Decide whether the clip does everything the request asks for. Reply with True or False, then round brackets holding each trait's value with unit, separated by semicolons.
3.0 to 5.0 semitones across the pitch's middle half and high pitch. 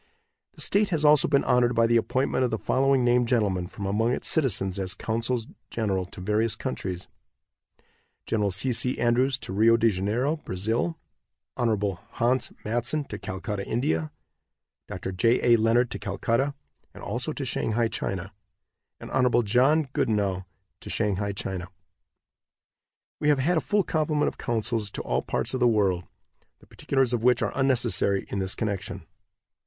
False (4.3 semitones; 115 Hz)